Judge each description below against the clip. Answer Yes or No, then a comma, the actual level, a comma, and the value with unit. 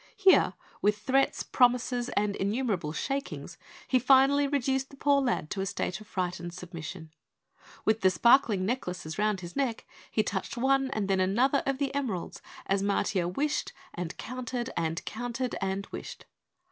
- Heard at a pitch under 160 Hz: No, high, 220 Hz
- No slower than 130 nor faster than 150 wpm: No, average, 160 wpm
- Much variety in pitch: Yes, wide, 5.9 semitones